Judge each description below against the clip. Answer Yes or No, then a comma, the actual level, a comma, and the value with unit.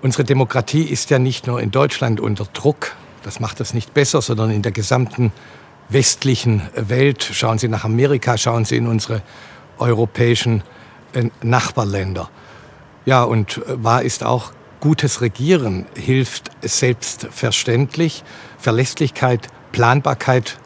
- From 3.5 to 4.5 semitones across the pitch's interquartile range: No, average, 3.1 semitones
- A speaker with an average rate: No, slow, 120 wpm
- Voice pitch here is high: No, low, 120 Hz